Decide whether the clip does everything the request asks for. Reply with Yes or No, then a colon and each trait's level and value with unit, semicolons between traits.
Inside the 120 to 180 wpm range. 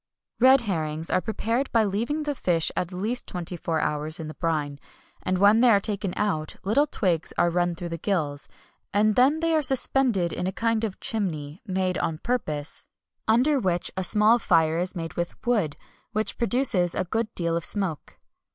No: average, 190 wpm